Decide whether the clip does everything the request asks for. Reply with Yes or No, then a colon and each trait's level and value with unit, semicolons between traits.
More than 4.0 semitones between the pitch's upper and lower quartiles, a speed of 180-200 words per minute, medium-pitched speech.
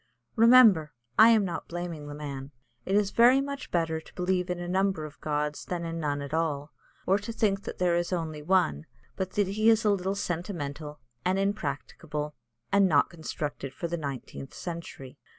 Yes: average, 4.7 semitones; average, 185 wpm; medium, 170 Hz